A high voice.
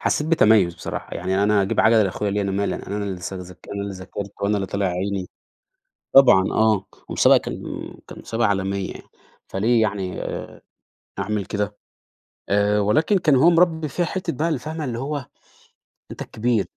No: low, 105 Hz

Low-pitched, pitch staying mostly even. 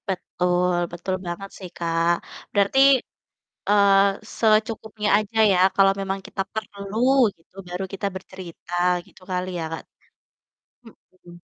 No: high, 195 Hz; narrow, 2.3 semitones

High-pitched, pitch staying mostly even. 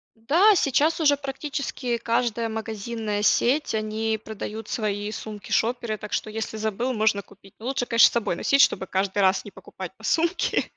No: high, 220 Hz; average, 3.1 semitones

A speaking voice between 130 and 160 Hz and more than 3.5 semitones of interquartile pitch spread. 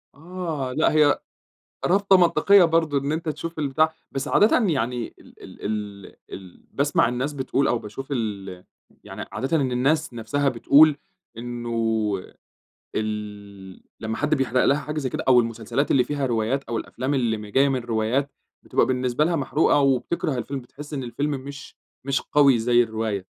Yes: low, 135 Hz; average, 4.2 semitones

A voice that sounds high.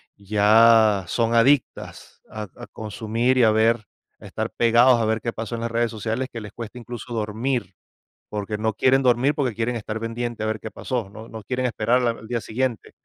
No: low, 115 Hz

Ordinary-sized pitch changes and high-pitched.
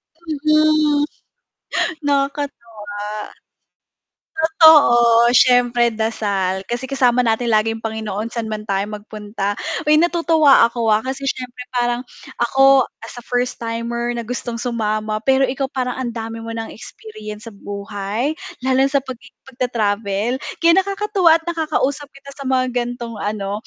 Yes: average, 3.8 semitones; high, 240 Hz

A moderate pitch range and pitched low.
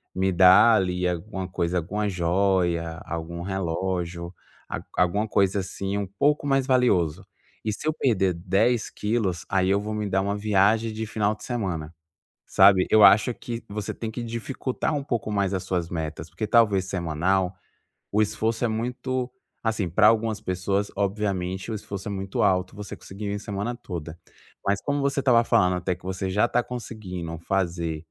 Yes: average, 3.3 semitones; low, 100 Hz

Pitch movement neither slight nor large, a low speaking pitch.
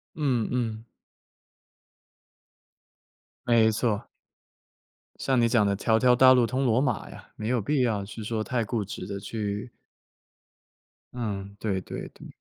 Yes: average, 3.1 semitones; low, 115 Hz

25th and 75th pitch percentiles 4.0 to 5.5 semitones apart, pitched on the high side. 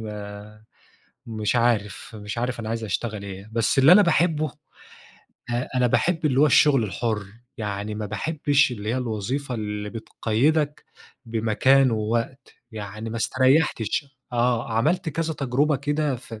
No: average, 4.4 semitones; low, 120 Hz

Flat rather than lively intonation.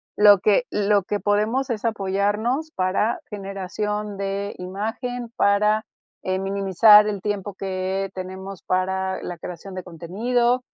Yes: narrow, 2.0 semitones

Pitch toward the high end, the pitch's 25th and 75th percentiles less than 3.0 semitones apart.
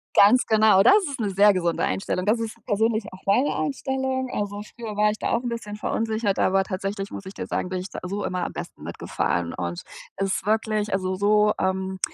Yes: high, 205 Hz; narrow, 2.6 semitones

